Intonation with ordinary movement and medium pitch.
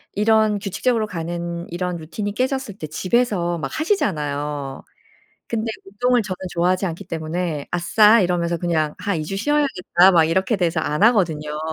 Yes: average, 4.5 semitones; medium, 180 Hz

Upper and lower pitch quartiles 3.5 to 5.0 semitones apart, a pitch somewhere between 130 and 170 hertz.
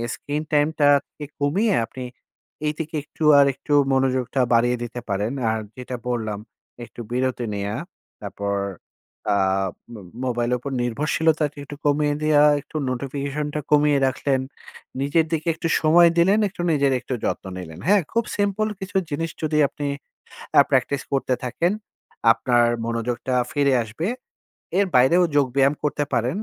Yes: average, 3.8 semitones; medium, 140 Hz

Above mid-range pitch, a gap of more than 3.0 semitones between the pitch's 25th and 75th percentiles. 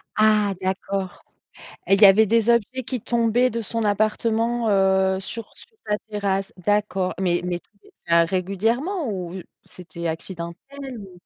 Yes: high, 205 Hz; average, 3.4 semitones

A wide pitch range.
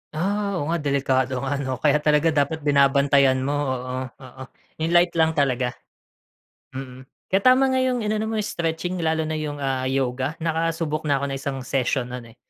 No: average, 3.7 semitones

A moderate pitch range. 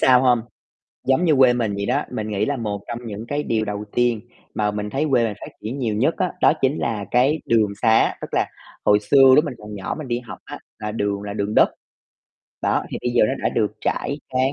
Yes: average, 3.9 semitones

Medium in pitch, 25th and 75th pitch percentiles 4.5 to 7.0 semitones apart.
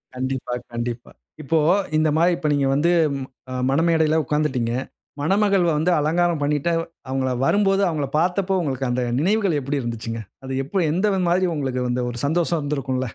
Yes: medium, 150 Hz; average, 4.8 semitones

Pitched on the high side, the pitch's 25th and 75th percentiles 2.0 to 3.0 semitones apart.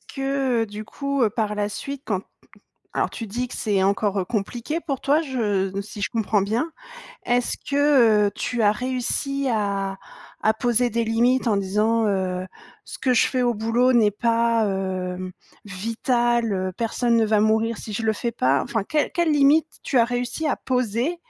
No: high, 230 Hz; average, 3.4 semitones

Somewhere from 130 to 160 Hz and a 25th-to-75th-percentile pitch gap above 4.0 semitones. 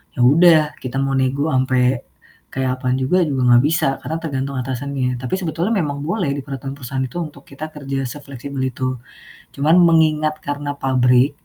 No: medium, 140 Hz; average, 2.8 semitones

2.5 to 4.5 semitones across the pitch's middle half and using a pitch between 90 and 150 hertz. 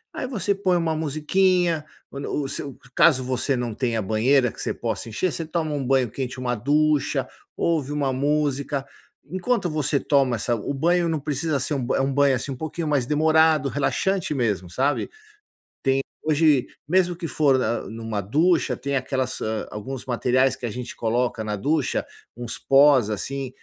Yes: average, 3.9 semitones; medium, 140 Hz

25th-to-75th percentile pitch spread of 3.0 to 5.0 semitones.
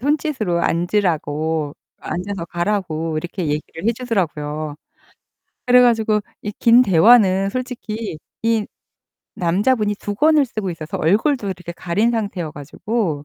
No: wide, 5.6 semitones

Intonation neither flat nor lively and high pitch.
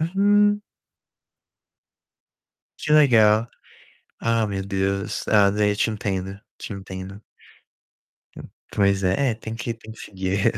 No: average, 3.0 semitones; low, 105 Hz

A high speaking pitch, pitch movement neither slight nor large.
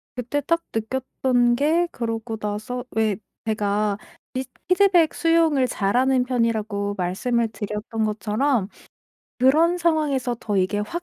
Yes: high, 240 Hz; average, 4.9 semitones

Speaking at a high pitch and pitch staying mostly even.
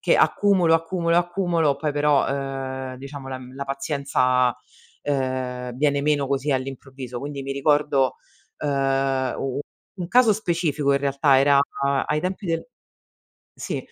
No: medium, 140 Hz; narrow, 2.3 semitones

